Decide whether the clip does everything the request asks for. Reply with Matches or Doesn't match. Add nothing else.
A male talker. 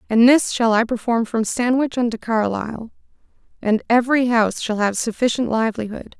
Doesn't match